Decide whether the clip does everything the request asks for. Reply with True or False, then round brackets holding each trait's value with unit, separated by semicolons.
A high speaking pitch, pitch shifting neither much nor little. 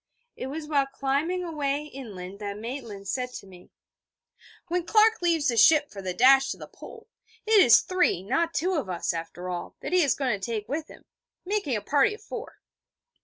False (275 Hz; 8.0 semitones)